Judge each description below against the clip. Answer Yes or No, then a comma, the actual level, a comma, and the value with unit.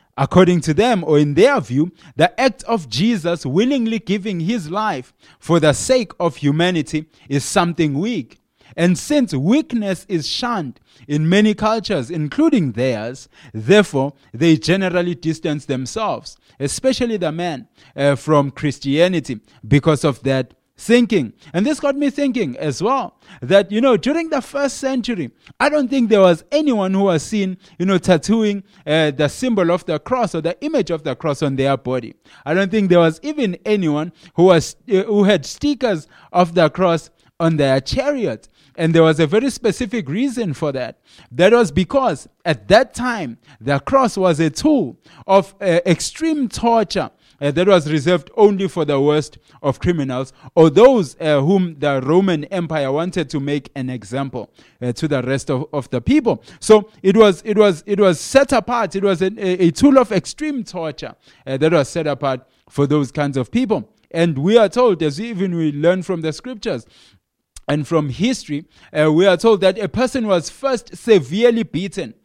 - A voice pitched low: No, medium, 175 Hz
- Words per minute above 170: Yes, average, 180 wpm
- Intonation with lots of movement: Yes, wide, 6.6 semitones